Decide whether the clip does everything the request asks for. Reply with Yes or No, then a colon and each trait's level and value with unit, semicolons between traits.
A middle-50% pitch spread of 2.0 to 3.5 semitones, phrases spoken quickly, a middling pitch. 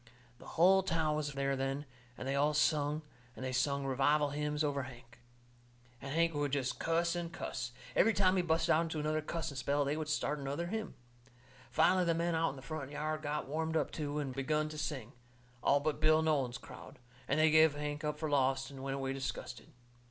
Yes: narrow, 2.5 semitones; fast, 210 wpm; medium, 150 Hz